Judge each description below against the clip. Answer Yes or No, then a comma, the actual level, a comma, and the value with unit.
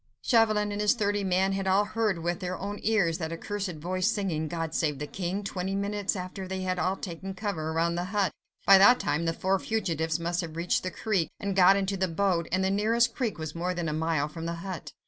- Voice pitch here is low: No, medium, 185 Hz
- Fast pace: Yes, fast, 240 wpm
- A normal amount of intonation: Yes, average, 3.1 semitones